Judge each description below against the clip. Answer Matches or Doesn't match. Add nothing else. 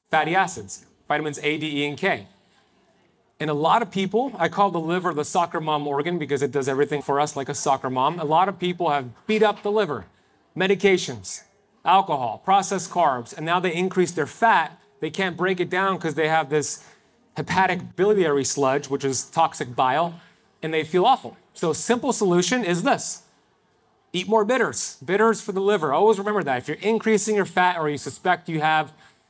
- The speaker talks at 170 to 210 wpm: Matches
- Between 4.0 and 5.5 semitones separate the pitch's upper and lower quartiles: Matches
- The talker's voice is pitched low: Doesn't match